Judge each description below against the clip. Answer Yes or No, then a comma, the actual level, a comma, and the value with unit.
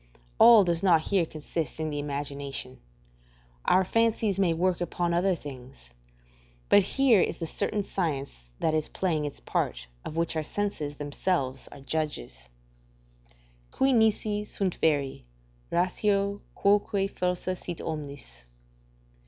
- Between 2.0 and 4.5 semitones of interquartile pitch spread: No, average, 5.2 semitones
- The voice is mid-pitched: Yes, medium, 170 Hz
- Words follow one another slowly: Yes, slow, 130 wpm